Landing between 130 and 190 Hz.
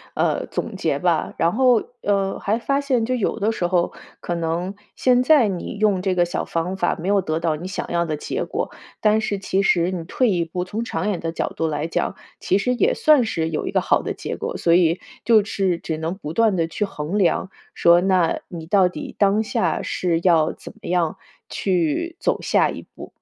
Yes: medium, 185 Hz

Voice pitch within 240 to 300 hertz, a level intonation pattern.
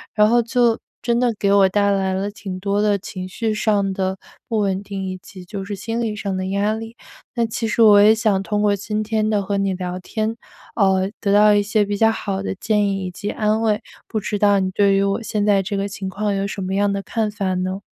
No: high, 205 Hz; narrow, 1.6 semitones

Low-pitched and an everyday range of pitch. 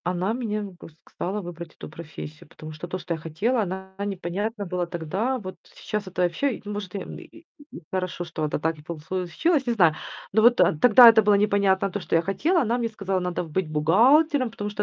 No: high, 190 Hz; average, 4.2 semitones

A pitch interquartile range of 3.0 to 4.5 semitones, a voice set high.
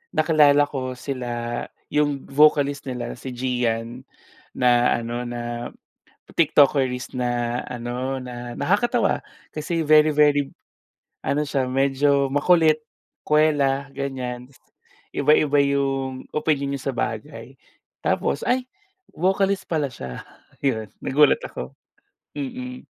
No: average, 3.4 semitones; low, 135 Hz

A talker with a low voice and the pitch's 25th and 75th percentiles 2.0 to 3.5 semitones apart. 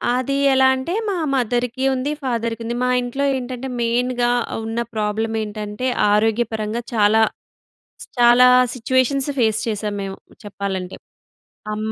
No: high, 235 Hz; average, 2.8 semitones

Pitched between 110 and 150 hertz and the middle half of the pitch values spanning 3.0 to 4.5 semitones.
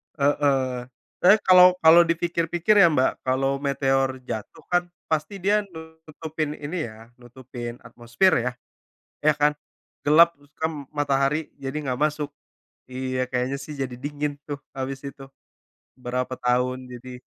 Yes: medium, 140 Hz; average, 3.3 semitones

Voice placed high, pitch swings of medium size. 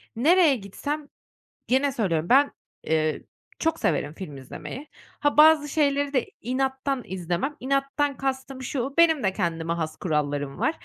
No: very high, 265 Hz; wide, 8.8 semitones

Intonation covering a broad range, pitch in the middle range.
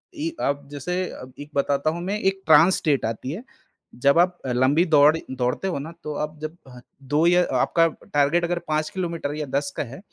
No: average, 3.6 semitones; medium, 155 Hz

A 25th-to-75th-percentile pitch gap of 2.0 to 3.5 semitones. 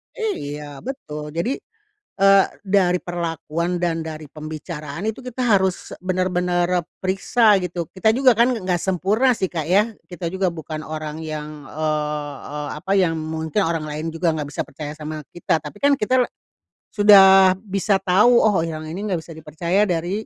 No: average, 4.0 semitones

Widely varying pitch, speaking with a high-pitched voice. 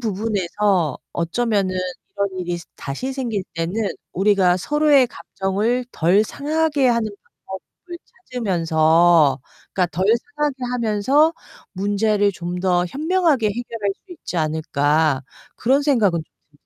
Yes: wide, 6.1 semitones; high, 200 Hz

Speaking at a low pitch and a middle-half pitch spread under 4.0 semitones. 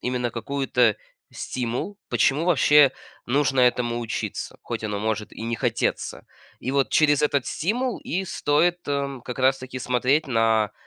Yes: low, 130 Hz; average, 3.6 semitones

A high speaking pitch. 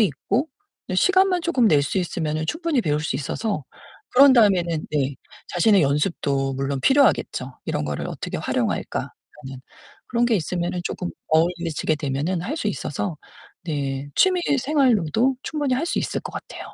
No: medium, 175 Hz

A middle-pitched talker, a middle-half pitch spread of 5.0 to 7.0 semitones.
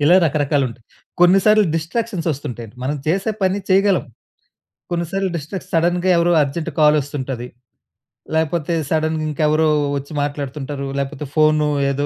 No: medium, 155 Hz; average, 3.5 semitones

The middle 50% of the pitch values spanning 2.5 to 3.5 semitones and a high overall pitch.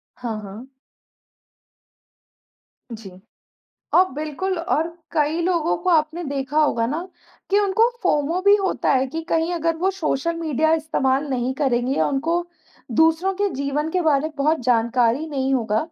No: average, 4.1 semitones; very high, 310 Hz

